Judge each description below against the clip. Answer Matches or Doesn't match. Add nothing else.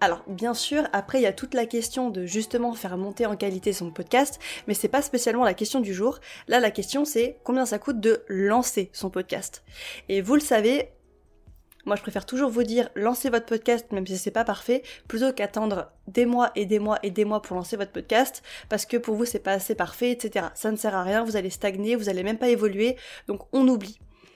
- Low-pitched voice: Doesn't match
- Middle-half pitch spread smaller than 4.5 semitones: Matches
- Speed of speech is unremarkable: Doesn't match